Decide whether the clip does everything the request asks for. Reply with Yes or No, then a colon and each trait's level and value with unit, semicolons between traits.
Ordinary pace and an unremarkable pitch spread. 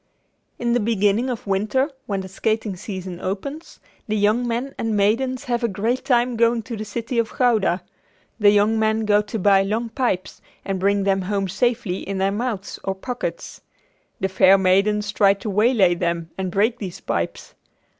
Yes: average, 180 wpm; average, 3.3 semitones